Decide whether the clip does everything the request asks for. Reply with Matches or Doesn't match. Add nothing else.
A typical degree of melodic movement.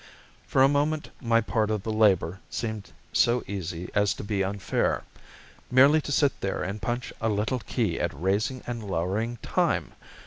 Matches